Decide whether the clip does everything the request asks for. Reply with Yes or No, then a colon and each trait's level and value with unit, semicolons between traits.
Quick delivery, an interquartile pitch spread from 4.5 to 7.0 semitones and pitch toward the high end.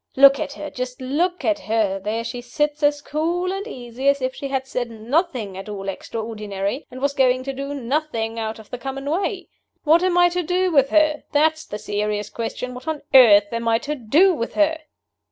Yes: fast, 210 wpm; average, 5.1 semitones; very high, 265 Hz